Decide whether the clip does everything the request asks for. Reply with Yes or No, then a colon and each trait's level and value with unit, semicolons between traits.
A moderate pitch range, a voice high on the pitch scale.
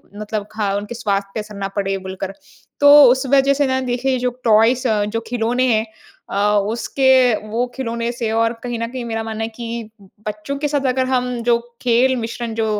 Yes: average, 3.0 semitones; high, 230 Hz